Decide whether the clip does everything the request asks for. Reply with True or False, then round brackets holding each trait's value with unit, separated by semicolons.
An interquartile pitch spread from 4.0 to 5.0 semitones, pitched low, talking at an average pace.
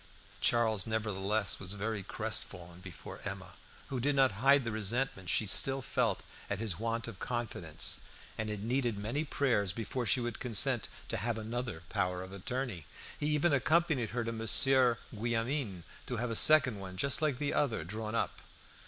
True (4.3 semitones; 115 Hz; 170 wpm)